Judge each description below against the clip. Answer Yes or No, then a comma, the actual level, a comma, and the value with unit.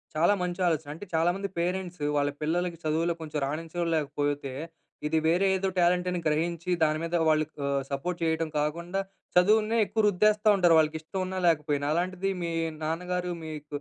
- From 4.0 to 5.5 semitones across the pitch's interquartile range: No, average, 2.7 semitones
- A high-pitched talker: No, medium, 170 Hz